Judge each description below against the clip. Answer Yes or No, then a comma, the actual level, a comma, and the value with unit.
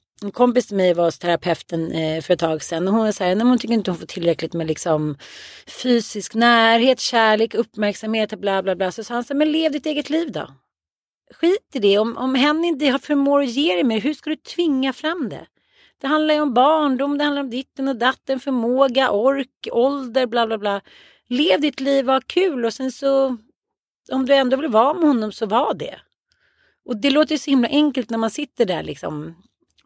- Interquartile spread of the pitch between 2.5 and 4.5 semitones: No, average, 4.9 semitones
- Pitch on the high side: Yes, very high, 250 Hz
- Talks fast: Yes, fast, 210 wpm